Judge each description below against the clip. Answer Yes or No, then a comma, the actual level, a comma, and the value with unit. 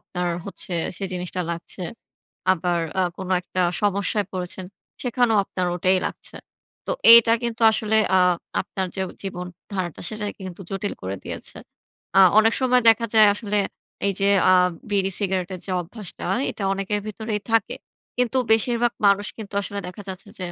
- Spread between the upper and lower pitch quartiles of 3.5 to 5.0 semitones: No, average, 2.9 semitones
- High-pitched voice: Yes, high, 200 Hz